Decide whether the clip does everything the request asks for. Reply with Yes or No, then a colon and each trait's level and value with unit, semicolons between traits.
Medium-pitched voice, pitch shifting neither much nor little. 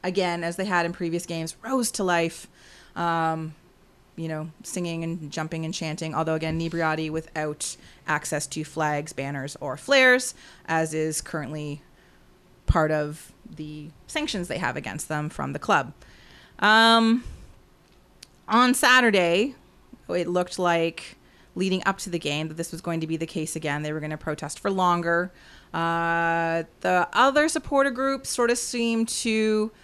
Yes: medium, 165 Hz; average, 3.8 semitones